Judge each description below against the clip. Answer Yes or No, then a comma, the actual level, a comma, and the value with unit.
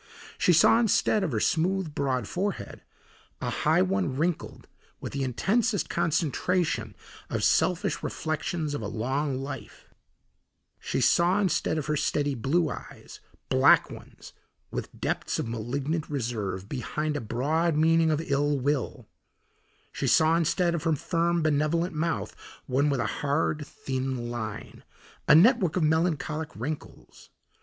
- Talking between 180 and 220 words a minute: No, average, 140 wpm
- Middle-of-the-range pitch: Yes, medium, 150 Hz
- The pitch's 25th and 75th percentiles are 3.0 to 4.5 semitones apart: Yes, average, 4.1 semitones